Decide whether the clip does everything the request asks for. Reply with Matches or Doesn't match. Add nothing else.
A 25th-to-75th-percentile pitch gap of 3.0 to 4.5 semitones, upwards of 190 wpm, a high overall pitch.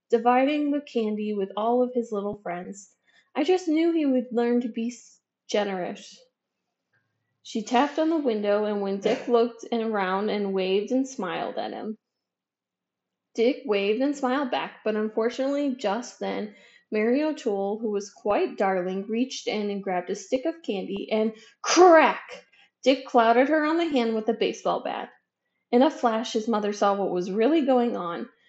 Doesn't match